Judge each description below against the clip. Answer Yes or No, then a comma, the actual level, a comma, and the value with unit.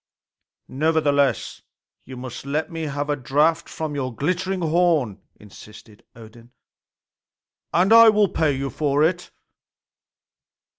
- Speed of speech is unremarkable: No, slow, 115 wpm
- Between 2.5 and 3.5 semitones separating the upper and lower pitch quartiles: No, average, 4.2 semitones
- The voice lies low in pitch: No, medium, 145 Hz